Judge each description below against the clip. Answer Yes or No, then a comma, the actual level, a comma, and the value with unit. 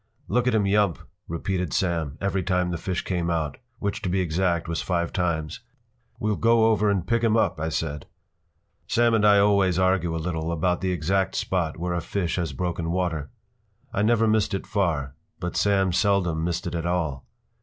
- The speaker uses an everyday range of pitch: Yes, average, 3.2 semitones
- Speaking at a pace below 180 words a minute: No, average, 195 wpm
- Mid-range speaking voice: No, very low, 90 Hz